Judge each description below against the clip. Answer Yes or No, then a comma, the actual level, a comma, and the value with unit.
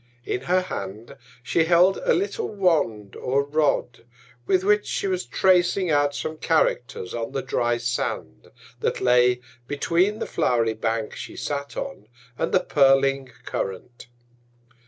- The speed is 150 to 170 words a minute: No, average, 140 wpm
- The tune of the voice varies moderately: No, wide, 6.8 semitones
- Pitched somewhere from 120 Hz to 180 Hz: Yes, medium, 140 Hz